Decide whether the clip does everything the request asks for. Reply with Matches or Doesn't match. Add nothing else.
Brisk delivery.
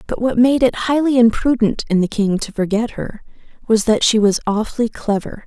Doesn't match